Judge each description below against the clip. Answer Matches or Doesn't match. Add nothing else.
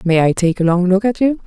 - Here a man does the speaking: Doesn't match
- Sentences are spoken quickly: Matches